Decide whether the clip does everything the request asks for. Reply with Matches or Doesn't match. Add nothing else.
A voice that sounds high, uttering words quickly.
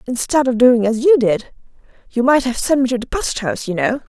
Matches